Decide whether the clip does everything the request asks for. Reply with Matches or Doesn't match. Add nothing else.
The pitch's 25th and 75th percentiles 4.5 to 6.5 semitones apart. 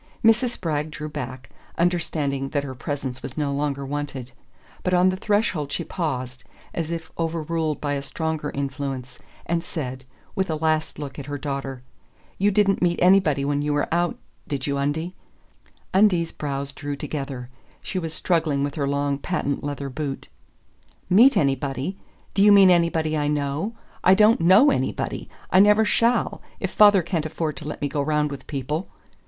Doesn't match